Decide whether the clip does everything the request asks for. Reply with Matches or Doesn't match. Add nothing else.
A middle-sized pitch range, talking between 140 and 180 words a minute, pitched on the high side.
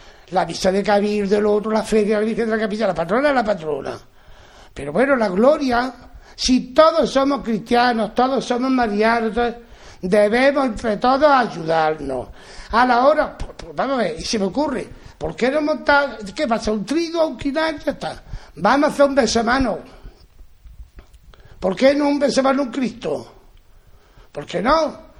Matches